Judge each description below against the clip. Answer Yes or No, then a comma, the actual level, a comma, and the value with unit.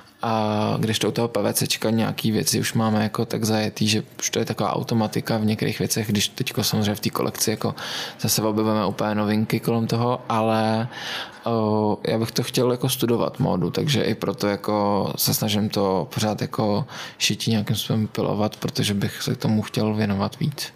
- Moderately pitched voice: No, low, 110 Hz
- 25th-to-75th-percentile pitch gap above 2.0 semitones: No, narrow, 1.7 semitones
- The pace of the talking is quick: Yes, fast, 180 wpm